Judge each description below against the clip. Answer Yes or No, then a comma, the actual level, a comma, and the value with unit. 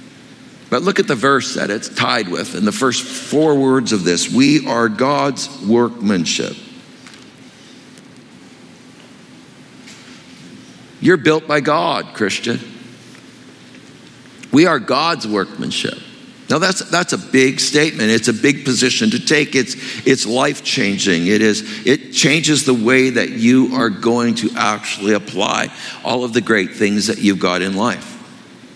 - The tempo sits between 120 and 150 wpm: Yes, average, 140 wpm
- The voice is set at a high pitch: No, low, 130 Hz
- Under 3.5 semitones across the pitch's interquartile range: No, average, 5.0 semitones